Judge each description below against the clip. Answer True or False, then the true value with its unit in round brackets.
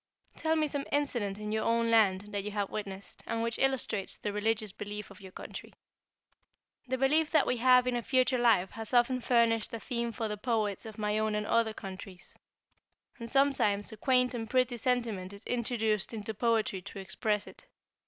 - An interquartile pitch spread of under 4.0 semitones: True (3.0 semitones)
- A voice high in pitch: True (225 Hz)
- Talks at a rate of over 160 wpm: True (195 wpm)